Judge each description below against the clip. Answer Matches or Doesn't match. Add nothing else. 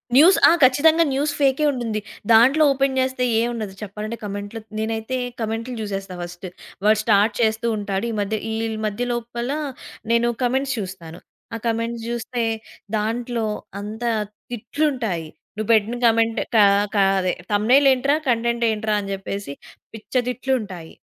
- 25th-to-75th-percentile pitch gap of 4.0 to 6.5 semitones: Doesn't match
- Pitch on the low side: Doesn't match